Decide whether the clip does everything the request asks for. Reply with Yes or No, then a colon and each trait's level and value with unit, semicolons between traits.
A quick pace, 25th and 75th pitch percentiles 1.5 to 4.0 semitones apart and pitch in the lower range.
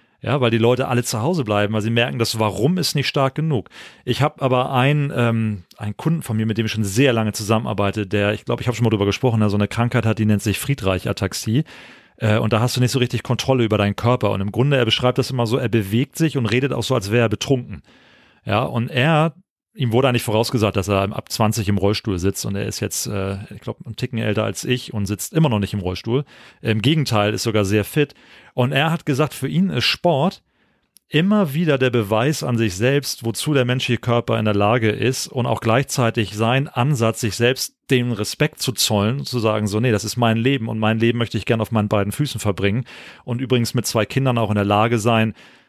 Yes: fast, 245 wpm; average, 3.4 semitones; low, 120 Hz